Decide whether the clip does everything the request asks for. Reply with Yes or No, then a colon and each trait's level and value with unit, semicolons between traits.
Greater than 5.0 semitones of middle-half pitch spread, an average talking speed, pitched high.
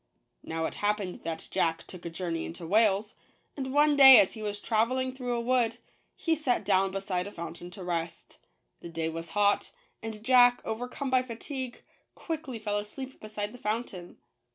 Yes: wide, 5.5 semitones; average, 180 wpm; high, 215 Hz